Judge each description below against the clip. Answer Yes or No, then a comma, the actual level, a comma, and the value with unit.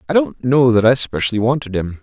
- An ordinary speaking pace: No, fast, 235 wpm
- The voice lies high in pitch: No, low, 115 Hz